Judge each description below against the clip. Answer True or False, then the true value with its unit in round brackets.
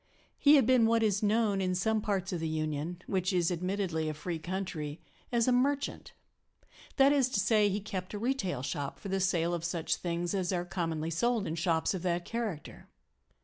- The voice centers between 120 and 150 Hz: False (185 Hz)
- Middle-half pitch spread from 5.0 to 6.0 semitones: False (4.2 semitones)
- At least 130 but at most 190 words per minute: False (200 wpm)